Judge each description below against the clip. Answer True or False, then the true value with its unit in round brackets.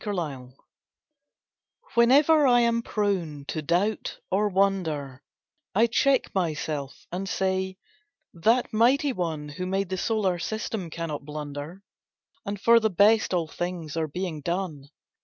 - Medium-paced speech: False (130 wpm)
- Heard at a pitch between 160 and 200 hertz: True (185 Hz)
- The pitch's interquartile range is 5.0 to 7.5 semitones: True (5.6 semitones)